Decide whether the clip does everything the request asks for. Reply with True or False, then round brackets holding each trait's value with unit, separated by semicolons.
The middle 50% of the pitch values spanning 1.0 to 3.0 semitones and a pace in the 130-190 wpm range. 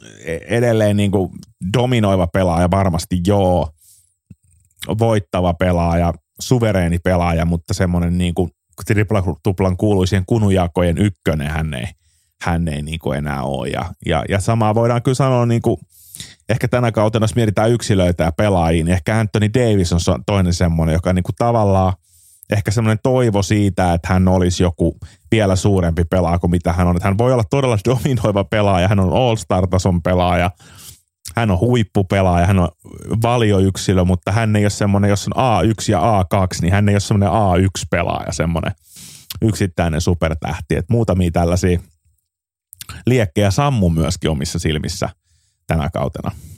False (3.4 semitones; 140 wpm)